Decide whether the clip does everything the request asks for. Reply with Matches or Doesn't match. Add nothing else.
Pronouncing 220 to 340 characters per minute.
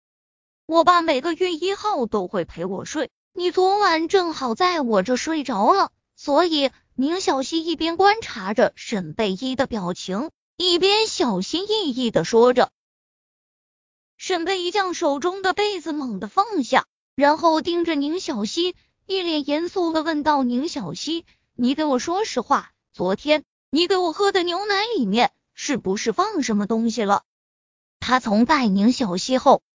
Matches